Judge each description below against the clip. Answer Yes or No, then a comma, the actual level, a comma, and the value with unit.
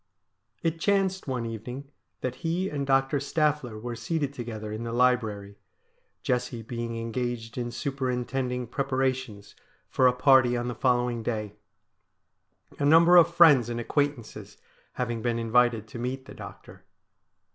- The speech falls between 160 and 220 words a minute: No, average, 145 wpm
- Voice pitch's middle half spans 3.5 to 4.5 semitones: No, average, 3.0 semitones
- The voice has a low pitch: Yes, low, 125 Hz